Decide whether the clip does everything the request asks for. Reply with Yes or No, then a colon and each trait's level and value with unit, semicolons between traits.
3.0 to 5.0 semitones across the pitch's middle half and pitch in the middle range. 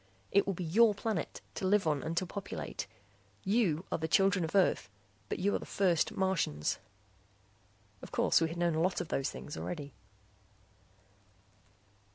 Yes: average, 3.5 semitones; medium, 180 Hz